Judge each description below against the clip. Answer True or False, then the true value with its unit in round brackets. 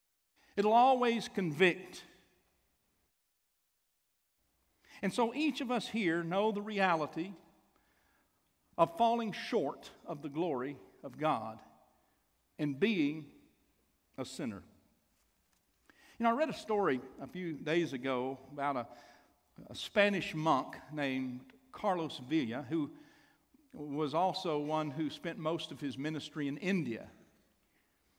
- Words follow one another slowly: True (115 wpm)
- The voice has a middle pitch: True (165 Hz)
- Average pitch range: False (6.8 semitones)